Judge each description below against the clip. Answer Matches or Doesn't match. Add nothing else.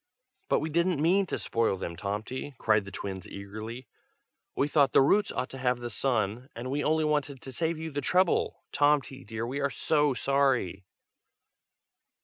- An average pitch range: Matches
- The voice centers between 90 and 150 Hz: Matches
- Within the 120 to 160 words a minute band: Doesn't match